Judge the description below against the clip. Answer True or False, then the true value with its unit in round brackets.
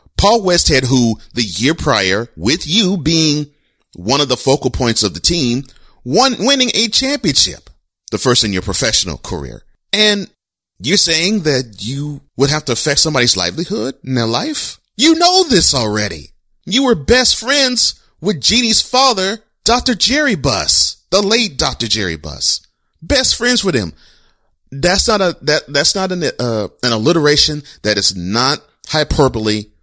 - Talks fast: False (155 wpm)